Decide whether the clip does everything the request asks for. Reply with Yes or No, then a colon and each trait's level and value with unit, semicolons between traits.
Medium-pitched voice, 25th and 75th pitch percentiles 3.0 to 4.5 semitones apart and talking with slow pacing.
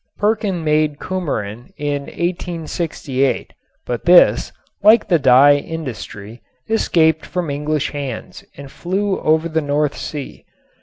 Yes: medium, 155 Hz; average, 3.7 semitones; slow, 115 wpm